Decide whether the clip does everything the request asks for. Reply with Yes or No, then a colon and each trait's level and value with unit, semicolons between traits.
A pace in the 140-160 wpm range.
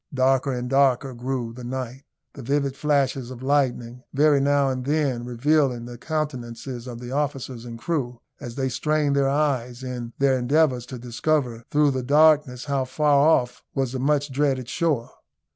No: average, 170 wpm